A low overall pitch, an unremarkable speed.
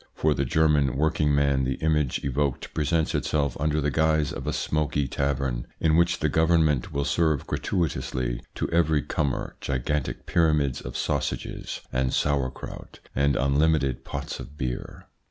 Yes: very low, 75 Hz; average, 150 wpm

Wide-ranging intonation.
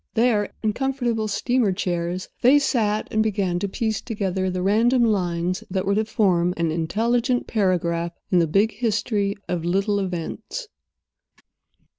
No: average, 3.9 semitones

